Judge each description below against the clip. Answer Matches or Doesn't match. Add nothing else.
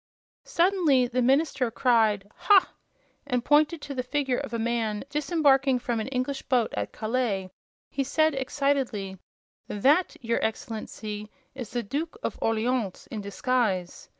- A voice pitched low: Doesn't match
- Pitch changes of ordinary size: Matches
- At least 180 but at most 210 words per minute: Doesn't match